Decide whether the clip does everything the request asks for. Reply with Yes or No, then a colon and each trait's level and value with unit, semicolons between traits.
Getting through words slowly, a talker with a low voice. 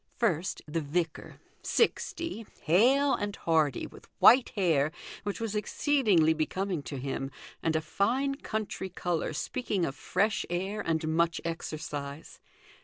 No: slow, 130 wpm; medium, 175 Hz